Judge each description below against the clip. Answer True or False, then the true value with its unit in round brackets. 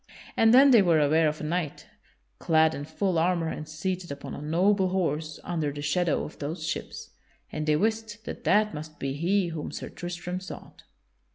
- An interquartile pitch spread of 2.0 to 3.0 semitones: False (3.4 semitones)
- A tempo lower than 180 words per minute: False (190 wpm)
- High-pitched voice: False (165 Hz)